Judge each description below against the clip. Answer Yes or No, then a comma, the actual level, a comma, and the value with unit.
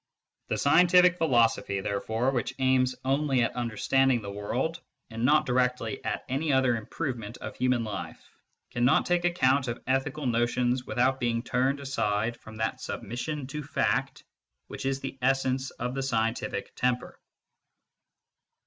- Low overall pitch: Yes, low, 130 Hz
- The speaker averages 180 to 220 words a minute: No, average, 140 wpm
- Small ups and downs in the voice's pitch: Yes, narrow, 2.3 semitones